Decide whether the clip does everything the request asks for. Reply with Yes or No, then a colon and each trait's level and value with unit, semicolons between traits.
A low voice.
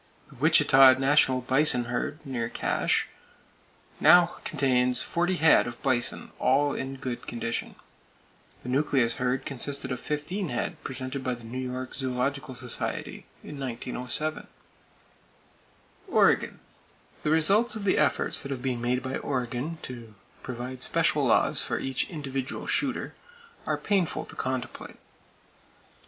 Yes: low, 130 Hz